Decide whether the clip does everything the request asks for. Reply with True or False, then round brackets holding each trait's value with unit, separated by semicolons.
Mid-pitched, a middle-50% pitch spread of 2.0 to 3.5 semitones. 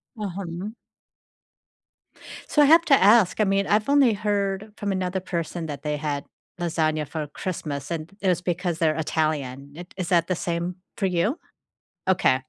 False (175 Hz; 4.0 semitones)